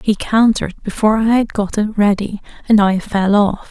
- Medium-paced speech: Yes, average, 180 wpm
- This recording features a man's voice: No, female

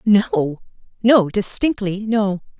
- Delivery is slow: Yes, slow, 70 wpm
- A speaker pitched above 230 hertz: No, high, 205 Hz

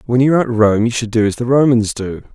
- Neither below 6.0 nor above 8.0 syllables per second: Yes, 6.6 syllables/s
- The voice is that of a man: Yes, male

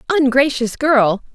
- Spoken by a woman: Yes, female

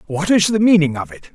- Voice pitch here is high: No, medium, 170 Hz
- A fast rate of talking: Yes, fast, 265 wpm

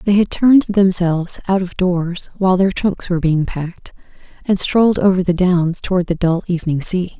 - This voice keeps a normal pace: Yes, average, 190 wpm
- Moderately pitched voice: Yes, medium, 180 Hz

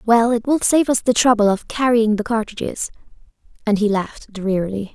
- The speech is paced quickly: No, average, 180 wpm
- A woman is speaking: Yes, female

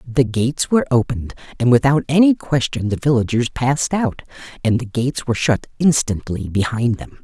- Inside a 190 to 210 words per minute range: No, average, 165 wpm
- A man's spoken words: Yes, male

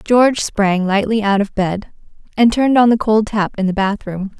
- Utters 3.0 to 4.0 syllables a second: No, 4.9 syllables/s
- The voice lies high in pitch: Yes, high, 210 Hz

